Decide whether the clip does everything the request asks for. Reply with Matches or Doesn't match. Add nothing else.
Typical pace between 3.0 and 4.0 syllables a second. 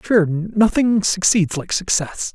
Matches